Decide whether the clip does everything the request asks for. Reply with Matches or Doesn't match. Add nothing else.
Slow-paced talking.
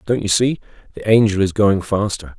Doesn't match